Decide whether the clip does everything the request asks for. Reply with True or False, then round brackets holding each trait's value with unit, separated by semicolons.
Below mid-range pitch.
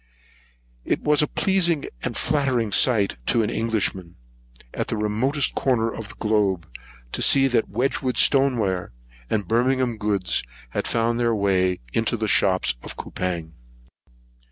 True (115 Hz)